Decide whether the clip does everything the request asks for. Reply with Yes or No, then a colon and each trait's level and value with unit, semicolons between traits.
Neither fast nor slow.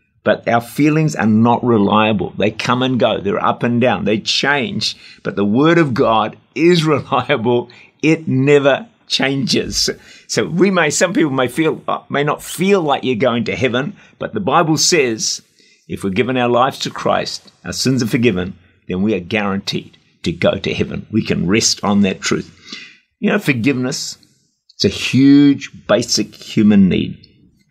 Yes: average, 170 wpm